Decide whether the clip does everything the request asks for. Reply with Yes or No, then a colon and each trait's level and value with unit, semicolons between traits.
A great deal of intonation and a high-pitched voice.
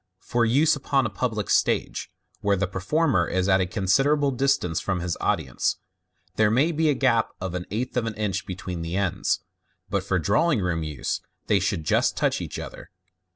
No: wide, 6.2 semitones; low, 100 Hz